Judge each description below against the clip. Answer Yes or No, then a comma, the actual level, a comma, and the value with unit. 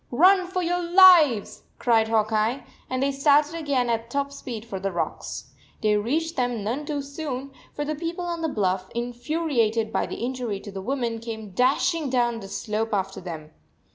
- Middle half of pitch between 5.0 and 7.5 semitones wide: Yes, wide, 5.4 semitones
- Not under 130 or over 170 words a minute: No, average, 185 wpm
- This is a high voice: Yes, high, 245 Hz